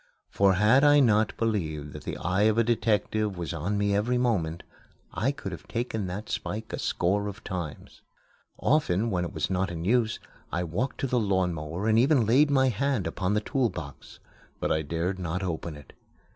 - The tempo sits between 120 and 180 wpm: No, average, 195 wpm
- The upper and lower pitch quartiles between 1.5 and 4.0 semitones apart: No, average, 4.8 semitones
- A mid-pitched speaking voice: No, low, 100 Hz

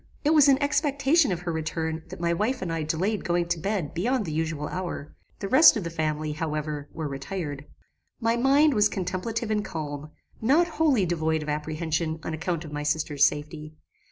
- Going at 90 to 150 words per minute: No, average, 190 wpm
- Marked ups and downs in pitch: Yes, wide, 6.2 semitones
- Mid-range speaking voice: Yes, medium, 170 Hz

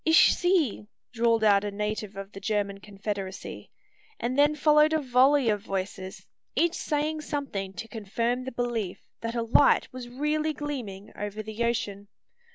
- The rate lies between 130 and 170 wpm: Yes, average, 160 wpm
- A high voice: Yes, high, 230 Hz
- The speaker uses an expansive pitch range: Yes, wide, 6.0 semitones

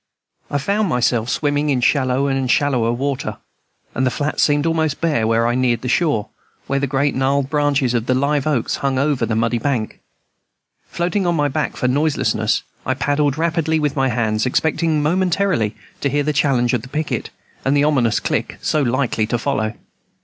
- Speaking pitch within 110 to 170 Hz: Yes, medium, 140 Hz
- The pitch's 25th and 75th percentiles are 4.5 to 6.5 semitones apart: No, average, 3.3 semitones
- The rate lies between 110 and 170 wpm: No, average, 190 wpm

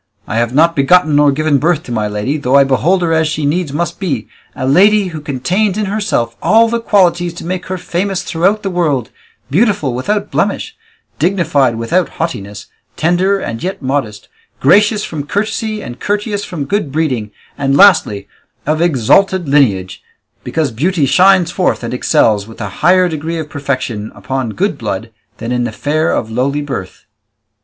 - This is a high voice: No, medium, 155 Hz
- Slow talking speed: No, average, 175 wpm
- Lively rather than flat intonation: Yes, wide, 6.3 semitones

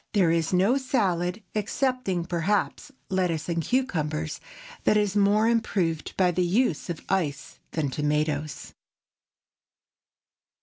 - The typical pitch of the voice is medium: Yes, medium, 180 Hz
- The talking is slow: Yes, slow, 115 wpm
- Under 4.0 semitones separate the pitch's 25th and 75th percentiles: No, average, 4.6 semitones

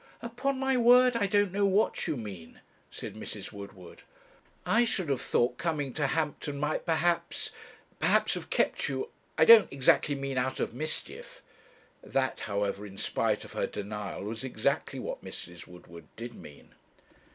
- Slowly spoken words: No, average, 160 wpm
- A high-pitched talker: No, medium, 140 Hz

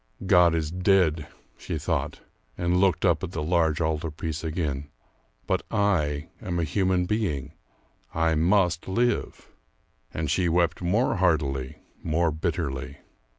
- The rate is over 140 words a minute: No, slow, 135 wpm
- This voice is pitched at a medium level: No, very low, 85 Hz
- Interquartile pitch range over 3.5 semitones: No, average, 3.0 semitones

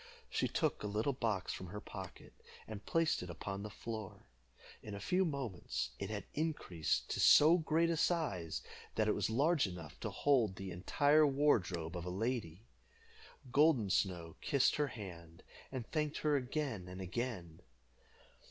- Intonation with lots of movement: Yes, wide, 7.9 semitones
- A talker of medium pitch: No, low, 110 Hz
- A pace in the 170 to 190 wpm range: No, average, 160 wpm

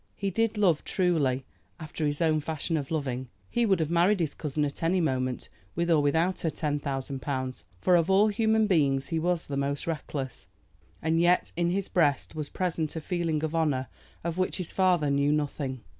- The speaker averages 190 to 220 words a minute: Yes, average, 200 wpm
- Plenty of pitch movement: No, average, 3.8 semitones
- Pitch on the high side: No, medium, 160 Hz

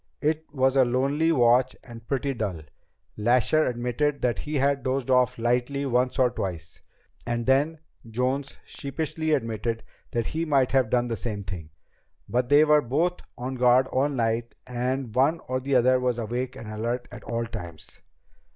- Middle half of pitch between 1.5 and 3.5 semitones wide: Yes, average, 2.8 semitones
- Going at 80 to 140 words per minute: No, average, 170 wpm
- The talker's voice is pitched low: Yes, low, 125 Hz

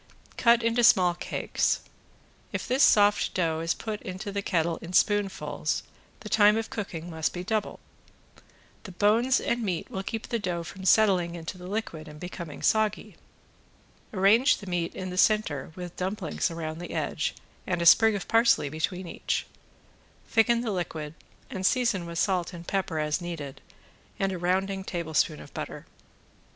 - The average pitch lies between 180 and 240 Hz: Yes, medium, 185 Hz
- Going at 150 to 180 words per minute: Yes, average, 165 wpm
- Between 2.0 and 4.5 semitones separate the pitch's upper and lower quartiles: Yes, average, 3.9 semitones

